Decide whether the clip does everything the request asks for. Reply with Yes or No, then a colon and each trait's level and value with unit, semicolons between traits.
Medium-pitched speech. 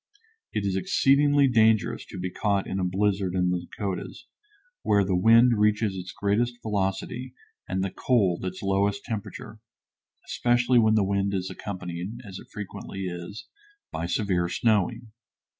No: low, 100 Hz